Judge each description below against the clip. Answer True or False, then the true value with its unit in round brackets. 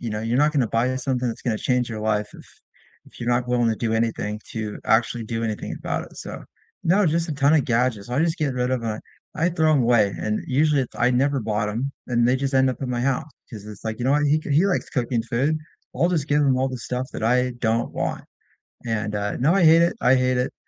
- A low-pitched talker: True (125 Hz)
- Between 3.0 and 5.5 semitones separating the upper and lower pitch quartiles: True (3.7 semitones)